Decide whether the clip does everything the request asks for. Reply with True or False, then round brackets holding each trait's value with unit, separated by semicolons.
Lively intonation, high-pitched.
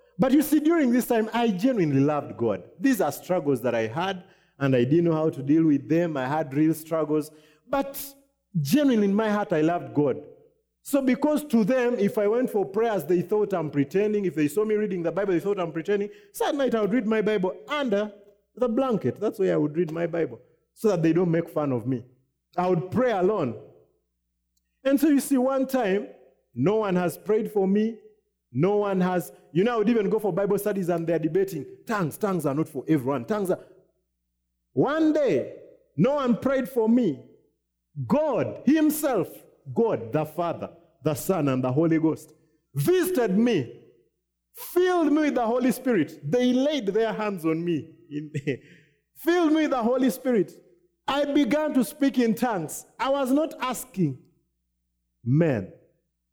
True (8.0 semitones; 200 Hz)